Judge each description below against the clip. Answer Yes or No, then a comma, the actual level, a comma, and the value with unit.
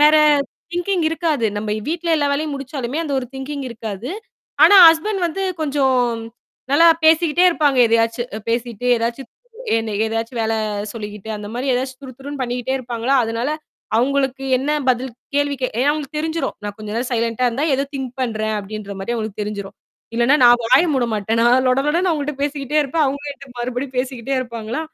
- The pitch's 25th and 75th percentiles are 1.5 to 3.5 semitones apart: No, average, 4.0 semitones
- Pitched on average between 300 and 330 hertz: No, very high, 255 Hz